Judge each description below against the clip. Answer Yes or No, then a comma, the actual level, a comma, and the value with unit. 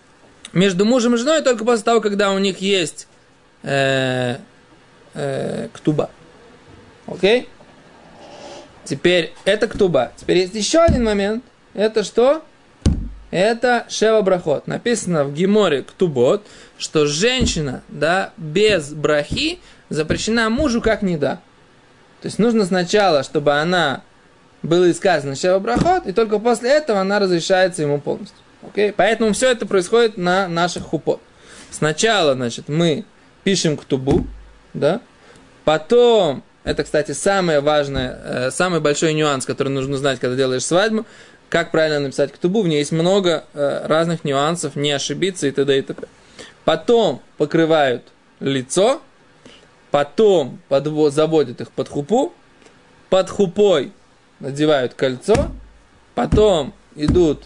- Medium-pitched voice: Yes, medium, 180 Hz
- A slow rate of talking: No, average, 125 wpm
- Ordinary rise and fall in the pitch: No, wide, 6.4 semitones